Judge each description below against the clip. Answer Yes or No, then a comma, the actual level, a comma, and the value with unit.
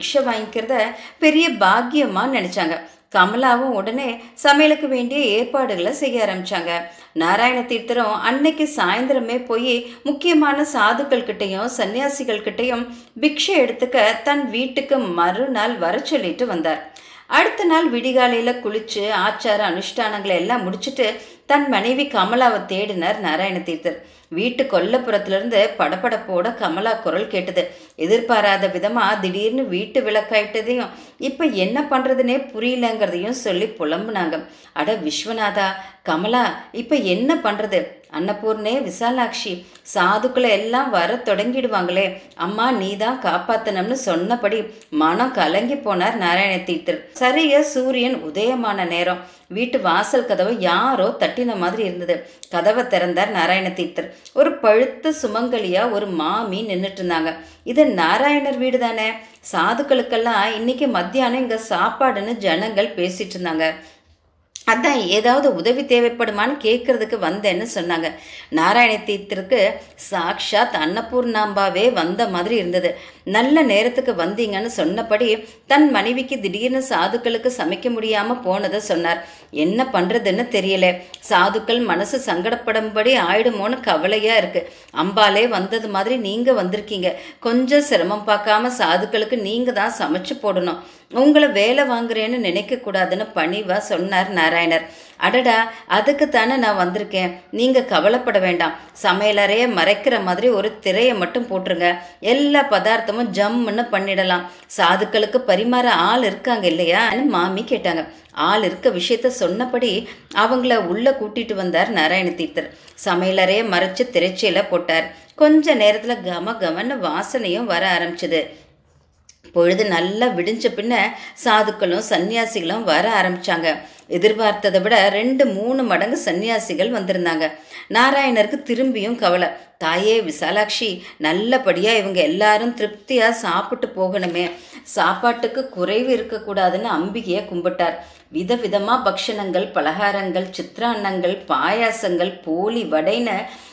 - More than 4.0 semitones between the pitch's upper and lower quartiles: Yes, average, 5.0 semitones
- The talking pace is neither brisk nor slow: Yes, average, 100 wpm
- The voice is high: Yes, high, 215 Hz